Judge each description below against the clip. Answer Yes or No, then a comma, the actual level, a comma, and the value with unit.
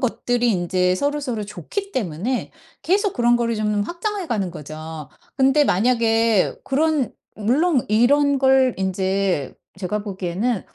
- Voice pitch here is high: Yes, high, 230 Hz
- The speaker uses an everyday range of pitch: No, wide, 6.0 semitones